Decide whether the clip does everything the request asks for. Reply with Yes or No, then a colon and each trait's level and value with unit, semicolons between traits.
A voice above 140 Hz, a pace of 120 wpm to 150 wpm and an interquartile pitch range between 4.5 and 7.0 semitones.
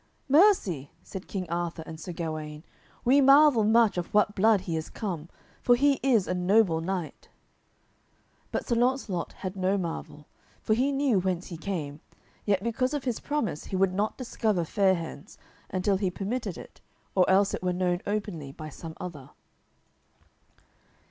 No: high, 190 Hz; average, 165 wpm; average, 4.8 semitones